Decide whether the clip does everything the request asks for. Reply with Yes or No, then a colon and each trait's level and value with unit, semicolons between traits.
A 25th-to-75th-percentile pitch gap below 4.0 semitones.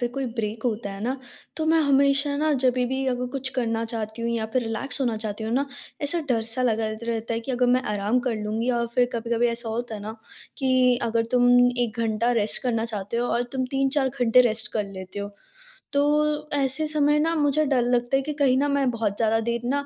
Yes: average, 3.2 semitones